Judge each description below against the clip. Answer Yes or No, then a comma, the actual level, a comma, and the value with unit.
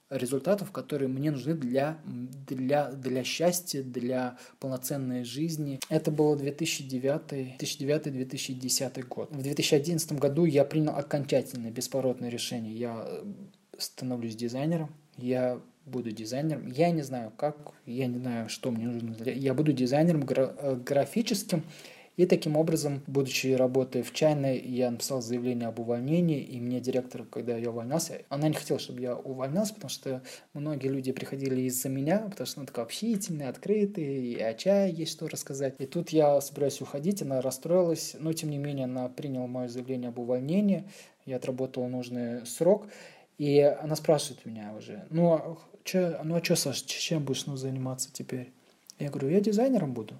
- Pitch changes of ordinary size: Yes, average, 3.7 semitones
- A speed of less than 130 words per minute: No, average, 155 wpm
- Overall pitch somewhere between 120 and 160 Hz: Yes, medium, 140 Hz